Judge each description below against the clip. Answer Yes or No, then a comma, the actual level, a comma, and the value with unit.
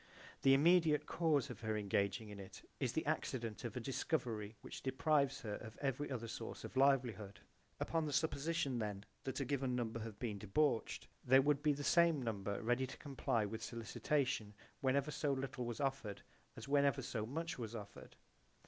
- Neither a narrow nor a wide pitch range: Yes, average, 4.2 semitones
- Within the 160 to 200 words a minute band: Yes, average, 180 wpm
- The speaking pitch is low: Yes, low, 130 Hz